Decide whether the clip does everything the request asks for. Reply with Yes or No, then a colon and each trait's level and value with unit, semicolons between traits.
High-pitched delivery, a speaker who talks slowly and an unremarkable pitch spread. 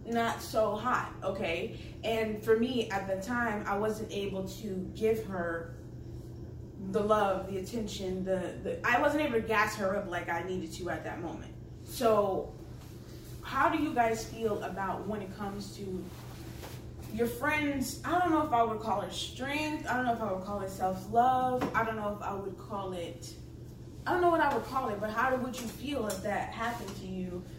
No: high, 215 Hz; fast, 205 wpm; average, 4.0 semitones